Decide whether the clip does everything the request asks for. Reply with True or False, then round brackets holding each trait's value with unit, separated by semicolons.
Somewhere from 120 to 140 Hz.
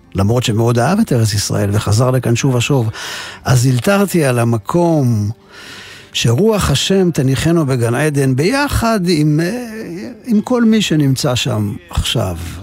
True (135 Hz)